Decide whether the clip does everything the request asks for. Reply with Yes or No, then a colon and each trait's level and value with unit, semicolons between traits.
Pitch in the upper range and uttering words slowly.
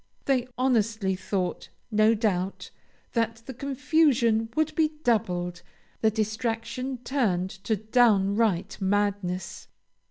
Yes: high, 220 Hz; slow, 100 wpm